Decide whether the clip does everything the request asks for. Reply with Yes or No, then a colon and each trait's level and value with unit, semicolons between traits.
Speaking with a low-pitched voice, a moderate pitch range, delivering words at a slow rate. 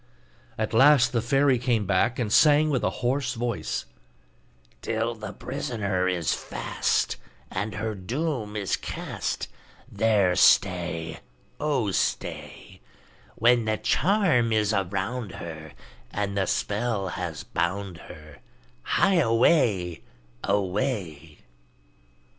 Yes: low, 110 Hz; average, 4.7 semitones; slow, 110 wpm